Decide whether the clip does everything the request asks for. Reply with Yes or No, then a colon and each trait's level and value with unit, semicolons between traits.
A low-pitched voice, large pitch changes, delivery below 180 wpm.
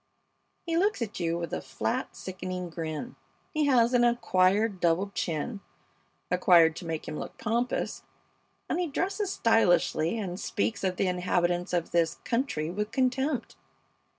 No: high, 190 Hz; wide, 5.9 semitones; average, 150 wpm